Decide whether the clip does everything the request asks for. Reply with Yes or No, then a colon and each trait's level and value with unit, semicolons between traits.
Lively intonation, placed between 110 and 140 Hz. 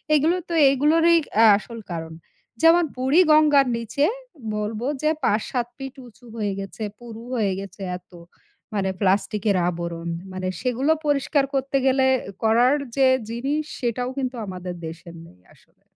No: wide, 5.8 semitones; high, 240 Hz